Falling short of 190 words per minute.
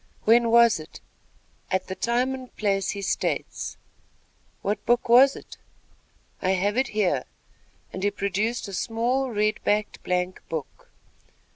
Yes: average, 140 wpm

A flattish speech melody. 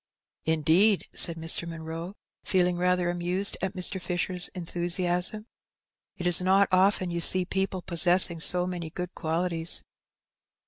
Yes: narrow, 1.5 semitones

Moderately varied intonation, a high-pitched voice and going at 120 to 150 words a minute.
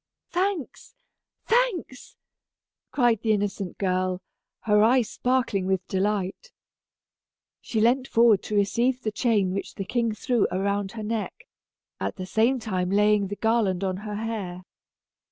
Yes: average, 3.6 semitones; high, 210 Hz; slow, 135 wpm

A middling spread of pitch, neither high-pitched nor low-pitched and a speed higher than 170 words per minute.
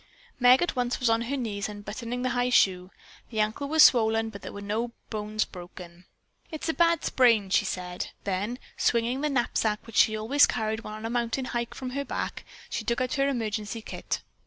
No: average, 3.1 semitones; high, 230 Hz; fast, 205 wpm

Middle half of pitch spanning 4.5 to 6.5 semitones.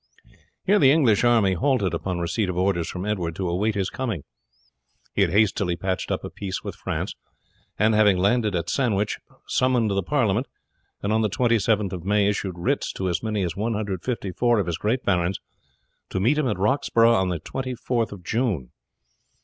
No: average, 4.0 semitones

